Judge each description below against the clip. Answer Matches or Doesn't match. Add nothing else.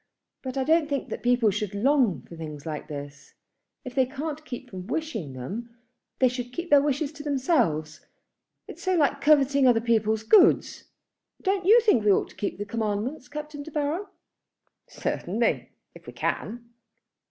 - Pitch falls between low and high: Doesn't match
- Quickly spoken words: Doesn't match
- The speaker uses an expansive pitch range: Matches